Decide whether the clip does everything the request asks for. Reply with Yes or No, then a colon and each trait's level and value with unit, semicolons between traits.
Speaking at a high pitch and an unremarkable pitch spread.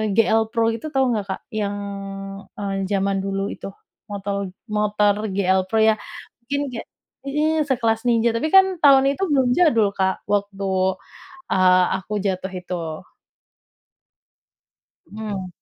Yes: high, 215 Hz; average, 4.0 semitones